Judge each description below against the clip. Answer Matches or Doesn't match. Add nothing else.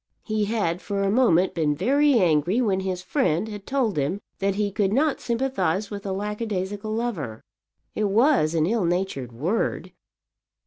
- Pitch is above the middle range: Matches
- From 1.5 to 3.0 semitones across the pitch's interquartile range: Doesn't match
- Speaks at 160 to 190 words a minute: Matches